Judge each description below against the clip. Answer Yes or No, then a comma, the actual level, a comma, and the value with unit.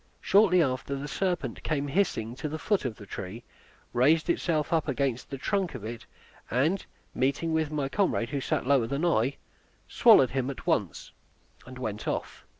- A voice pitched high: No, medium, 140 Hz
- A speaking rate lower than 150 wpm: No, average, 175 wpm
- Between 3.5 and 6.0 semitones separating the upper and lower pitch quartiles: Yes, average, 4.4 semitones